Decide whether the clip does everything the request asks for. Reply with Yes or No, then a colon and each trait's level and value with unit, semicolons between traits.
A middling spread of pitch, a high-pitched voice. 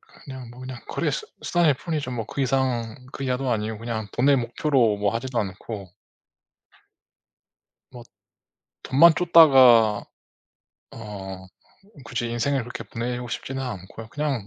No: average, 3.2 semitones; low, 125 Hz